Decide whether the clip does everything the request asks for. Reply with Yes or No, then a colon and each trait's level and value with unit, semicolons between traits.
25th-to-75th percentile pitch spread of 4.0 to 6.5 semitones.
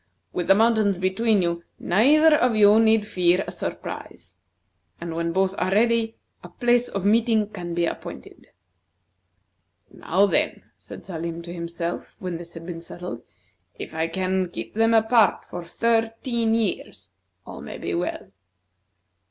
Yes: average, 4.7 semitones